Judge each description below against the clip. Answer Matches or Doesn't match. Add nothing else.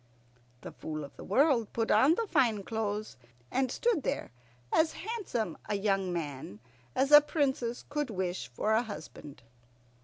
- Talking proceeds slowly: Doesn't match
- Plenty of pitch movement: Matches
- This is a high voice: Matches